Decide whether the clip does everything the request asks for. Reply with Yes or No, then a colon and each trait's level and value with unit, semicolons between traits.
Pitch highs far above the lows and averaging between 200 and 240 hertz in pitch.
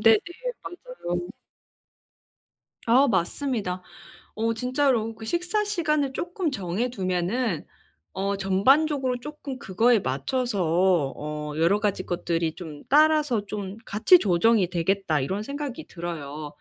Yes: wide, 7.3 semitones; high, 210 Hz